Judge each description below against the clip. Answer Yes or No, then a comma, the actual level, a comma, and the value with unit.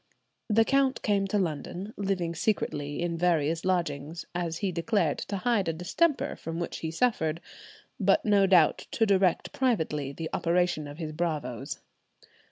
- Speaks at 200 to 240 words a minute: No, average, 155 wpm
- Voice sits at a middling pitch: Yes, medium, 175 Hz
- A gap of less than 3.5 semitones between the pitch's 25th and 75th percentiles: No, average, 3.9 semitones